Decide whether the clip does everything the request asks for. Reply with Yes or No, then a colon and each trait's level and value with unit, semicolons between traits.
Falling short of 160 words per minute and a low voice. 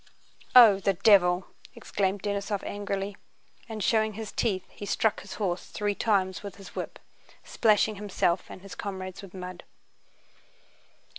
No: average, 140 wpm; high, 200 Hz